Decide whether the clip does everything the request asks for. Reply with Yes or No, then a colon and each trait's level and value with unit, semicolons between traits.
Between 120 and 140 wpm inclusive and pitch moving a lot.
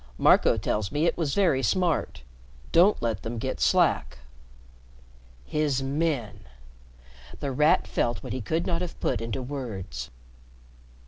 Yes: slow, 135 wpm; wide, 6.7 semitones